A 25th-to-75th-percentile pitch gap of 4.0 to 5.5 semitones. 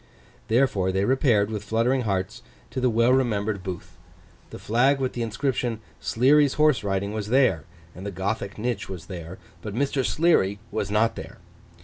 Yes: average, 4.4 semitones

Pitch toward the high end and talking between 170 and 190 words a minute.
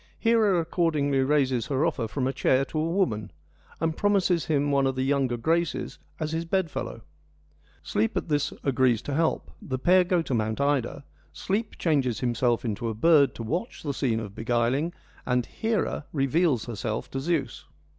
No: medium, 140 Hz; average, 175 wpm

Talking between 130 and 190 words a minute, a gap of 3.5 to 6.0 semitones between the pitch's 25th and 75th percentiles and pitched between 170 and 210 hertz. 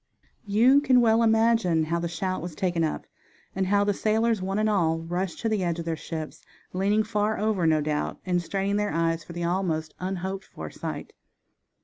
No: average, 200 wpm; average, 4.1 semitones; high, 190 Hz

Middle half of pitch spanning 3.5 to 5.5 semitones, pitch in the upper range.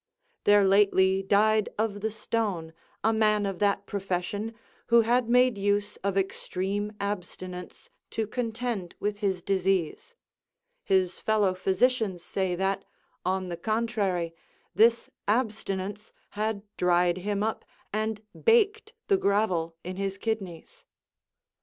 No: average, 2.7 semitones; high, 205 Hz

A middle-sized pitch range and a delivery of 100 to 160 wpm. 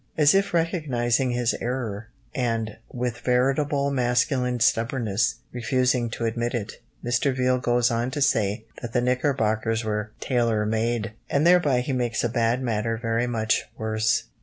No: narrow, 2.2 semitones; average, 150 wpm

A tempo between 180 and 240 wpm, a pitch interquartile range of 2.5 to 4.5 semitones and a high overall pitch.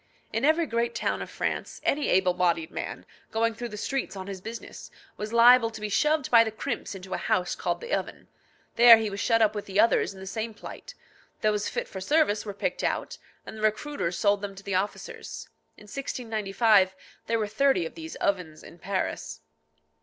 Yes: average, 200 wpm; average, 3.1 semitones; high, 215 Hz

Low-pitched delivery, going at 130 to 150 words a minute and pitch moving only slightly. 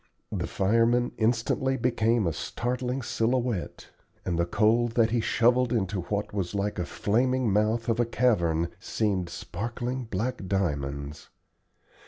No: low, 110 Hz; slow, 135 wpm; average, 4.0 semitones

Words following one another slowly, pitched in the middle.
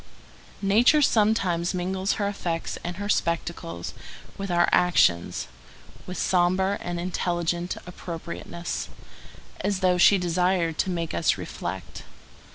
Yes: slow, 115 wpm; medium, 180 Hz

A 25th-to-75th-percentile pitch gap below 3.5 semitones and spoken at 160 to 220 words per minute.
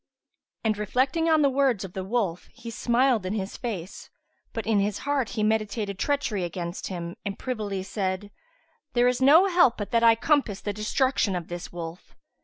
No: average, 4.8 semitones; average, 190 wpm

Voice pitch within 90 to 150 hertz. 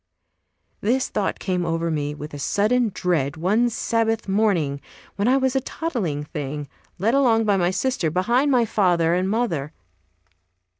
No: high, 195 Hz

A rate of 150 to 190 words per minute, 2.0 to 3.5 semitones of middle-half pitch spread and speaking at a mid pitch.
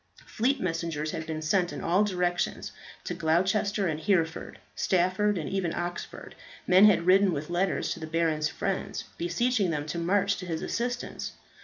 Yes: average, 165 wpm; average, 3.2 semitones; medium, 180 Hz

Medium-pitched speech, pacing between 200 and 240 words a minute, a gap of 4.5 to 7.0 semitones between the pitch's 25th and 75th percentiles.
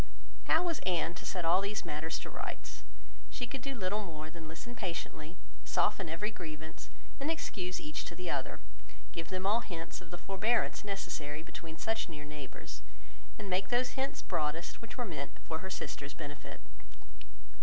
No: medium, 180 Hz; average, 175 wpm; average, 4.9 semitones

